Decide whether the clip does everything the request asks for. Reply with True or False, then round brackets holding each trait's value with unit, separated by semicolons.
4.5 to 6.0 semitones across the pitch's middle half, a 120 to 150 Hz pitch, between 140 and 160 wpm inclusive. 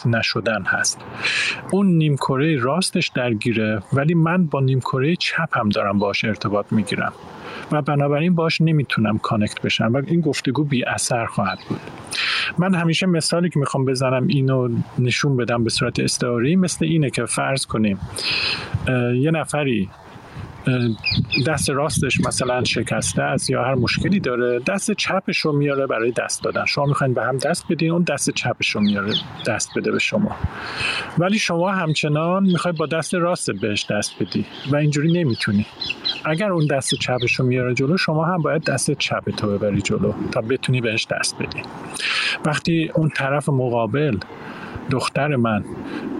True (5.1 semitones; 140 Hz; 155 wpm)